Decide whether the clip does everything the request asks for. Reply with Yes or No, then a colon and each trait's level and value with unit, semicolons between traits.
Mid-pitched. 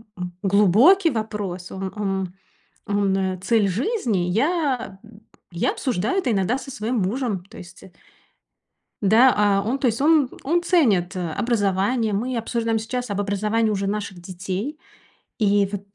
No: high, 210 Hz